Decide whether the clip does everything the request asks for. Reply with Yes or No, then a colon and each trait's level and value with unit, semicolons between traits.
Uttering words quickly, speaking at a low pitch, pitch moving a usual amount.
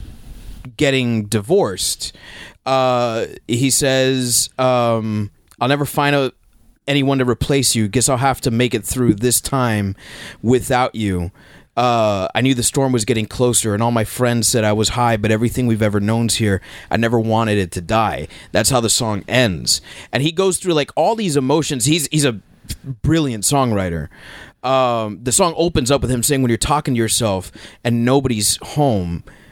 No: average, 175 wpm; low, 120 Hz; average, 3.8 semitones